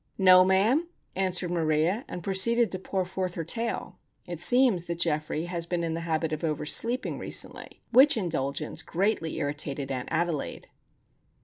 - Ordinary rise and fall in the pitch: Yes, average, 3.4 semitones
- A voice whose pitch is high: No, medium, 175 Hz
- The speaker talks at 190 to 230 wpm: No, average, 155 wpm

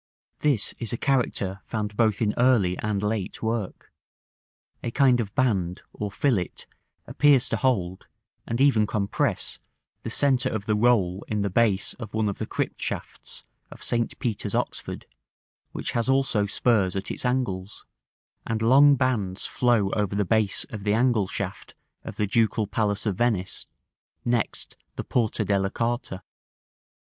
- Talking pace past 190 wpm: No, average, 155 wpm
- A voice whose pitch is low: Yes, low, 110 Hz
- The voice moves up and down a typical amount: Yes, average, 3.3 semitones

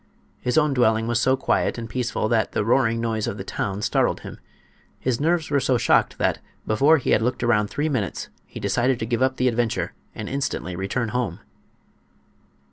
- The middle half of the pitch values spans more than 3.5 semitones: No, average, 3.0 semitones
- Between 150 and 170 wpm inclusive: No, average, 195 wpm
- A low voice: Yes, low, 120 Hz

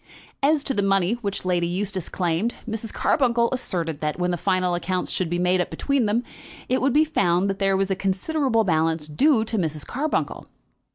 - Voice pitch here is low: No, high, 195 Hz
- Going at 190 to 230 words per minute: Yes, average, 195 wpm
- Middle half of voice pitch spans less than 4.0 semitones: No, average, 5.1 semitones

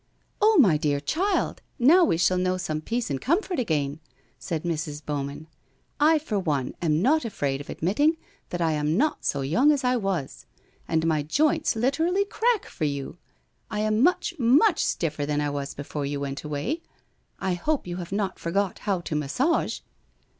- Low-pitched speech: No, medium, 180 Hz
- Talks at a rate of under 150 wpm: No, average, 190 wpm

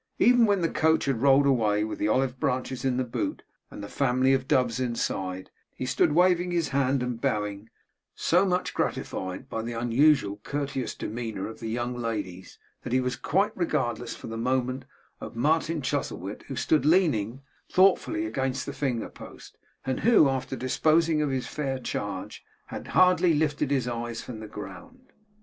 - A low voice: Yes, low, 130 Hz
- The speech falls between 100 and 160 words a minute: No, average, 175 wpm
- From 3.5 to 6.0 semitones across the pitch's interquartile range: Yes, average, 4.7 semitones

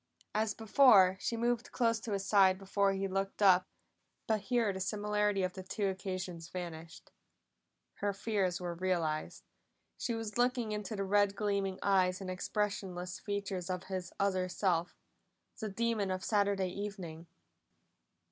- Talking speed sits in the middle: Yes, average, 145 wpm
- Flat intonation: Yes, narrow, 2.1 semitones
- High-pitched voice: Yes, high, 195 Hz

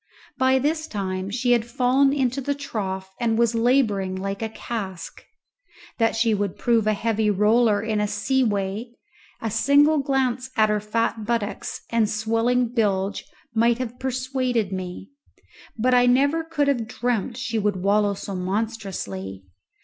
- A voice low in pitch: No, high, 225 Hz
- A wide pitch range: No, average, 3.6 semitones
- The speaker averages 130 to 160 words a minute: Yes, average, 155 wpm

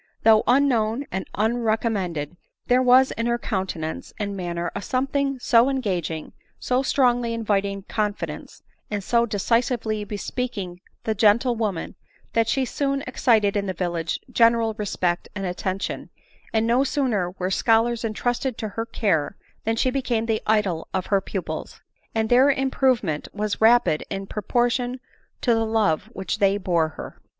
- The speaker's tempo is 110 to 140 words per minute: No, average, 150 wpm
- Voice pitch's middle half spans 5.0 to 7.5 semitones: No, average, 3.8 semitones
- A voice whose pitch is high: Yes, high, 220 Hz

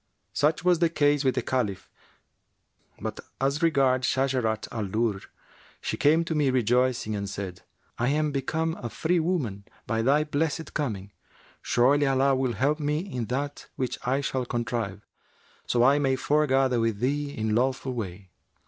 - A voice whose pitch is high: No, low, 130 Hz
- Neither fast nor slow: Yes, average, 160 wpm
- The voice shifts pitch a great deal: No, average, 4.0 semitones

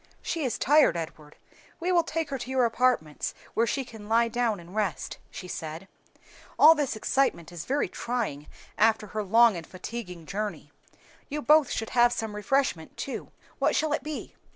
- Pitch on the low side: No, high, 230 Hz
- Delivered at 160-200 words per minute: Yes, average, 175 wpm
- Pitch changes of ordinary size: No, wide, 6.2 semitones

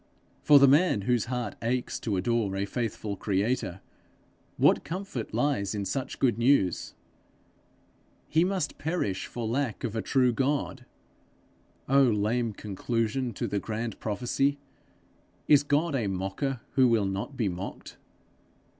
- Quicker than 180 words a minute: No, slow, 135 wpm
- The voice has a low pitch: Yes, low, 120 Hz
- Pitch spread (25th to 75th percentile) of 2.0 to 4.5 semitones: No, average, 4.9 semitones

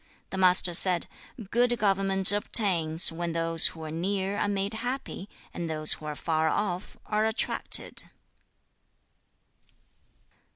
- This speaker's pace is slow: Yes, slow, 130 wpm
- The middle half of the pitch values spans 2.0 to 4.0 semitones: Yes, average, 3.6 semitones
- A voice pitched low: No, medium, 185 Hz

